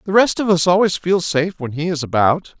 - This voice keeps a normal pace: No, fast, 255 wpm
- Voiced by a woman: No, male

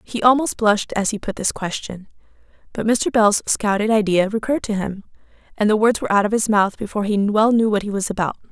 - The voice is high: Yes, high, 210 Hz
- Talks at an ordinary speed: No, fast, 225 wpm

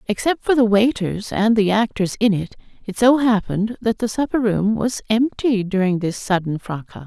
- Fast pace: No, average, 185 wpm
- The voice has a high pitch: Yes, high, 215 Hz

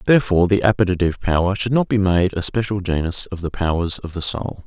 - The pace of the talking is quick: Yes, fast, 220 wpm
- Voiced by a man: Yes, male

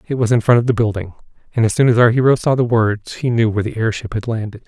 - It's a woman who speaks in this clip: No, male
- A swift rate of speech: Yes, fast, 295 wpm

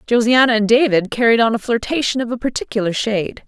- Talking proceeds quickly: No, average, 190 wpm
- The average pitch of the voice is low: No, high, 230 Hz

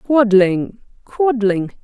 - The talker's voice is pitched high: Yes, high, 220 Hz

